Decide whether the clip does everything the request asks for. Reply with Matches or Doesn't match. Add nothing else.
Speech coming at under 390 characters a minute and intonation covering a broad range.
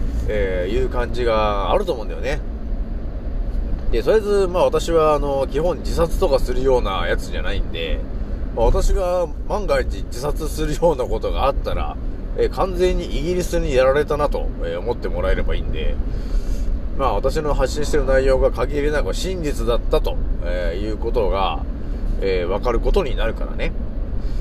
Matches